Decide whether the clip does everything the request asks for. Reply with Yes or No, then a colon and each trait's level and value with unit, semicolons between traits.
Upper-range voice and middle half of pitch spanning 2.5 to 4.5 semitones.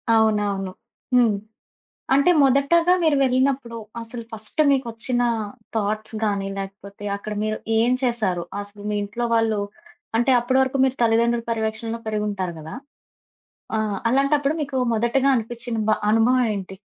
Yes: high, 230 Hz; average, 3.5 semitones